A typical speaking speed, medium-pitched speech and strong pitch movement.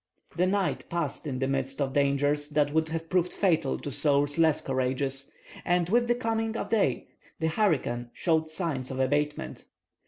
No: average, 175 wpm; medium, 150 Hz; average, 4.1 semitones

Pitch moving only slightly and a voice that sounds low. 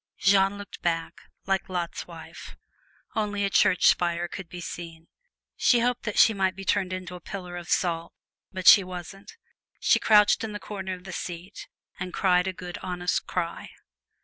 No: narrow, 2.0 semitones; medium, 185 Hz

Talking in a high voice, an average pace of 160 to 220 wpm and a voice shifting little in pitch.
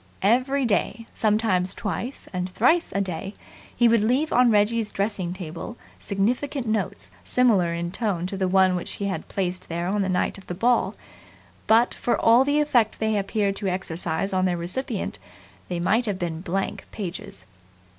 No: high, 200 Hz; average, 175 wpm; average, 4.2 semitones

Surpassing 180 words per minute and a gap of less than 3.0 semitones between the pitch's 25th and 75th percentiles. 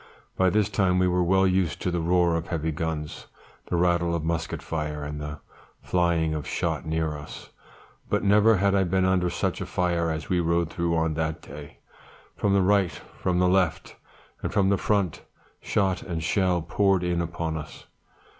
Yes: average, 190 wpm; narrow, 2.6 semitones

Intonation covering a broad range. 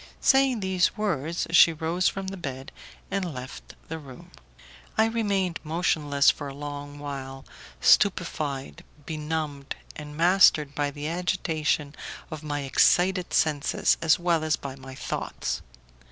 No: average, 3.9 semitones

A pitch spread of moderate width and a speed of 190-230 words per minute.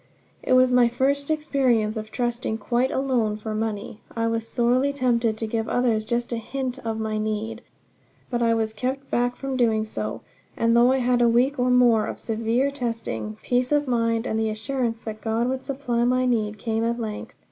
No: narrow, 2.3 semitones; average, 200 wpm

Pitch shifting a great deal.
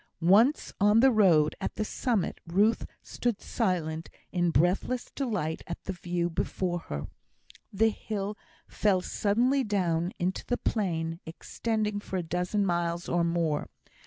No: average, 4.1 semitones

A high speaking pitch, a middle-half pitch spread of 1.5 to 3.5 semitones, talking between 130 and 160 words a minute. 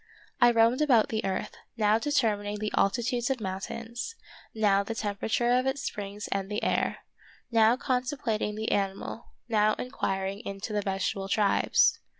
Yes: high, 220 Hz; average, 3.0 semitones; average, 150 wpm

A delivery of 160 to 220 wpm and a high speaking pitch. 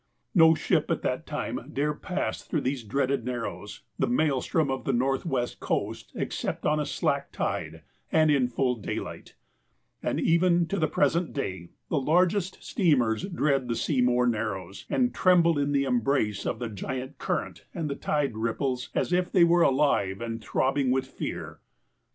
No: average, 165 wpm; low, 135 Hz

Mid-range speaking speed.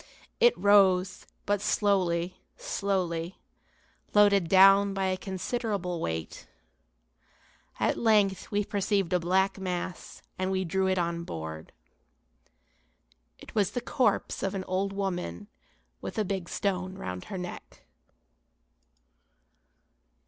No: slow, 115 wpm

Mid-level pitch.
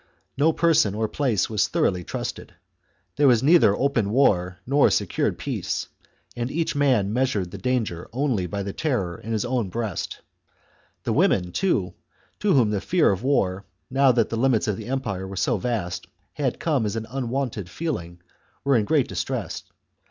No: low, 115 Hz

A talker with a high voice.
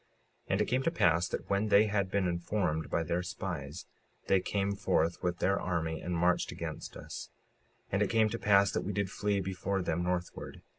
No: very low, 95 Hz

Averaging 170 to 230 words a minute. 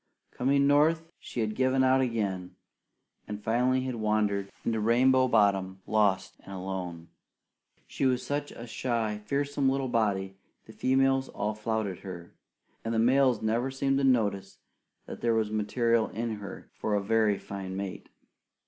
No: average, 155 wpm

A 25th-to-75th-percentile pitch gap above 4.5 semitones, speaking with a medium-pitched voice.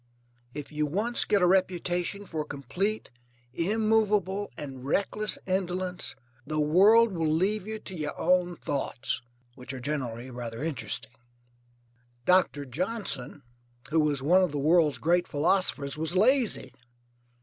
Yes: average, 5.1 semitones; medium, 175 Hz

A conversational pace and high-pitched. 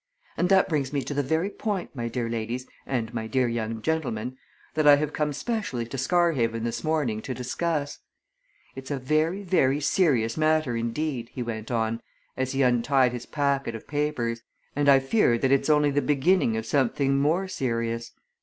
No: average, 180 wpm; low, 135 Hz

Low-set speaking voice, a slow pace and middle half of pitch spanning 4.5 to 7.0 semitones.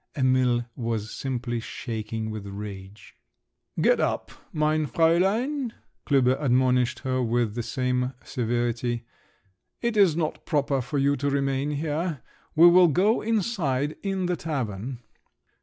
Yes: low, 130 Hz; slow, 125 wpm; average, 5.1 semitones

